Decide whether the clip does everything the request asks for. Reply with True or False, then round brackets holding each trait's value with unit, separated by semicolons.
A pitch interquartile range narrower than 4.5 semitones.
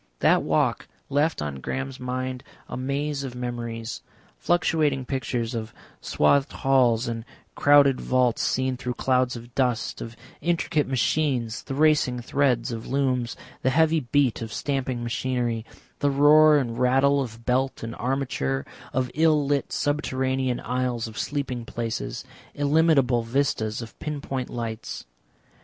True (2.9 semitones)